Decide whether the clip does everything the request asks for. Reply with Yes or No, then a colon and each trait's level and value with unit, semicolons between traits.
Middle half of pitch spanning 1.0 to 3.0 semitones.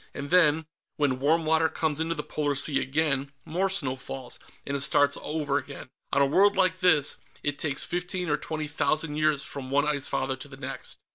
Yes: narrow, 2.5 semitones